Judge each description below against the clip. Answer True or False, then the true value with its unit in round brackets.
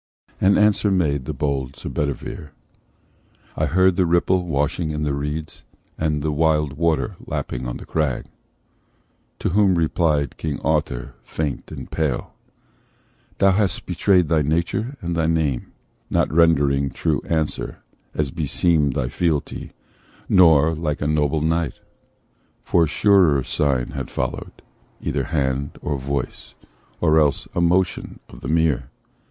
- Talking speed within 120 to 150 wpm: True (140 wpm)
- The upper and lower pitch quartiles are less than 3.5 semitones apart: True (3.0 semitones)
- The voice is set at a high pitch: False (75 Hz)